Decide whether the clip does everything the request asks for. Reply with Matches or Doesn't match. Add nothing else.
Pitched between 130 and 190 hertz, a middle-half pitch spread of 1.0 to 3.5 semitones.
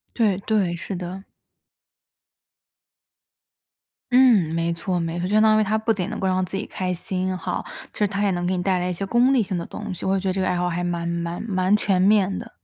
Matches